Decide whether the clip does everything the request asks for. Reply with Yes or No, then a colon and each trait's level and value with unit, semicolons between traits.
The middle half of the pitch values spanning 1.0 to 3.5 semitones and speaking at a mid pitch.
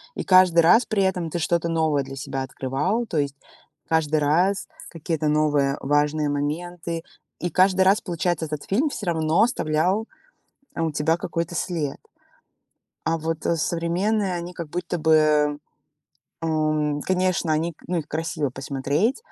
Yes: average, 3.0 semitones; medium, 165 Hz